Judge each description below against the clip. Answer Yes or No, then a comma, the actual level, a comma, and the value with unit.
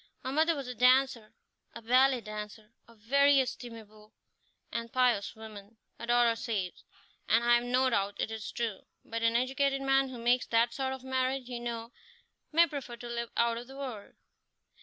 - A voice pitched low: No, high, 240 Hz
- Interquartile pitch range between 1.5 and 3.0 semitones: Yes, narrow, 2.4 semitones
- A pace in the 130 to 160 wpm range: No, average, 180 wpm